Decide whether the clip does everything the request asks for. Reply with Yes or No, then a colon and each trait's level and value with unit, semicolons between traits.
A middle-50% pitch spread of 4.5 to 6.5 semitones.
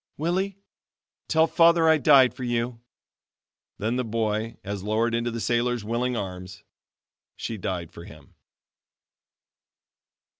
No: average, 3.5 semitones